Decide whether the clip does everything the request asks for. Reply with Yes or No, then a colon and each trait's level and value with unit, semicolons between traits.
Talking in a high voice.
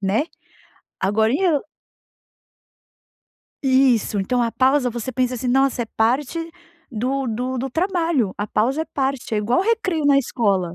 Yes: very high, 255 Hz